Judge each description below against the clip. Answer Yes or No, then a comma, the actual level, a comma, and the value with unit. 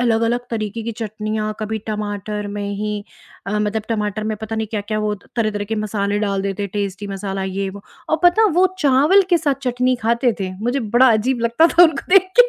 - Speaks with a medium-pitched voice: No, high, 215 Hz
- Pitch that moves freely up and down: No, average, 2.9 semitones